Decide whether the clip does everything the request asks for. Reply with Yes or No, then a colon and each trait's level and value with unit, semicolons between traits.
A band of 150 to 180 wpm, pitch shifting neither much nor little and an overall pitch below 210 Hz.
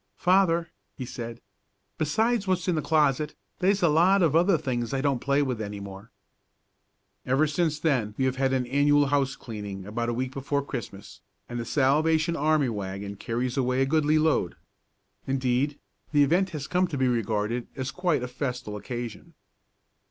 Yes: average, 175 wpm; average, 4.5 semitones; low, 135 Hz